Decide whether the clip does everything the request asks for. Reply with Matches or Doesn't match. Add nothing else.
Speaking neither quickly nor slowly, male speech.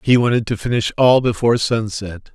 Matches